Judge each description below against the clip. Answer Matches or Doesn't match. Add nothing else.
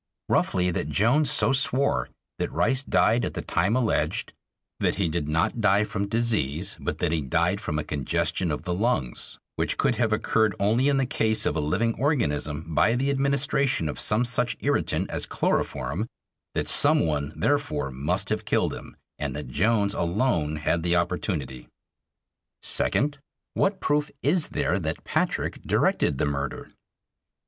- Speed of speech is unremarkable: Matches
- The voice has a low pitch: Matches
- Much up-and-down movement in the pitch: Matches